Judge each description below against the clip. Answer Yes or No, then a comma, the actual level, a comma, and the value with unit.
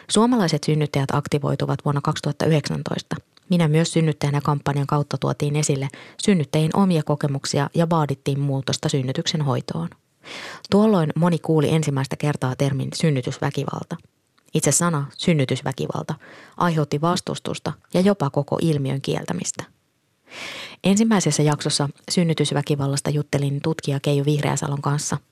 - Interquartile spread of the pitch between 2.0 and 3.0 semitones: Yes, narrow, 2.4 semitones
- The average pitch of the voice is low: No, medium, 150 Hz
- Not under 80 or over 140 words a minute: Yes, average, 105 wpm